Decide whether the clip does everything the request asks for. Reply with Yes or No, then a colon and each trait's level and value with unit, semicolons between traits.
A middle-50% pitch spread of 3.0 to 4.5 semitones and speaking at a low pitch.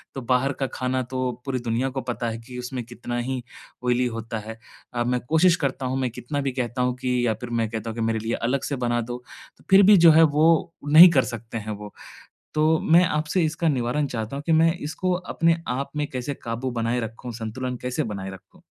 Yes: average, 3.9 semitones; low, 125 Hz